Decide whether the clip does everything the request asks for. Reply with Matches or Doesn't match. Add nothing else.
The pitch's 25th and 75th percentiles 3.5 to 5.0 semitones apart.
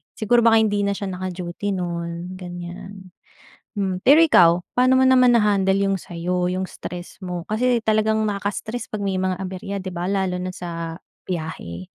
Doesn't match